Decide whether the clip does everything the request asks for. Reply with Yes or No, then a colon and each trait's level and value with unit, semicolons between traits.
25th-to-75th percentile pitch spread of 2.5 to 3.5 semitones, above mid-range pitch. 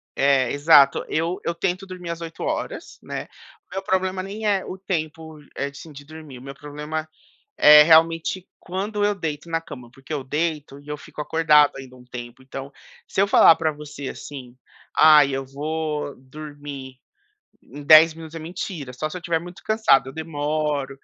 No: average, 2.9 semitones; medium, 155 Hz